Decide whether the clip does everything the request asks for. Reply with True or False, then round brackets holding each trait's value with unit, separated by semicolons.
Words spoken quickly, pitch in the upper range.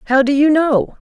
True (225 wpm; 280 Hz)